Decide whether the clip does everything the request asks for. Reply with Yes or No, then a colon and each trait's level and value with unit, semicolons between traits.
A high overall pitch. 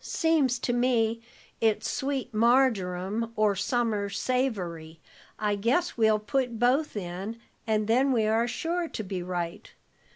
Yes: high, 225 Hz